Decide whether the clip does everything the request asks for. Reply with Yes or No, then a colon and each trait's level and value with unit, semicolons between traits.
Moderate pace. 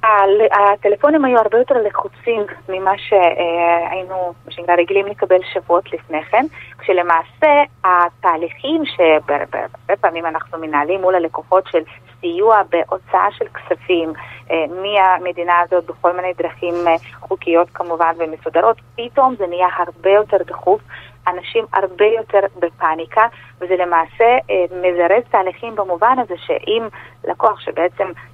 Yes: average, 110 wpm